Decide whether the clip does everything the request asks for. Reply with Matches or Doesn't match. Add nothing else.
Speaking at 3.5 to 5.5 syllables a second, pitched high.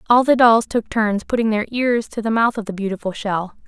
Matches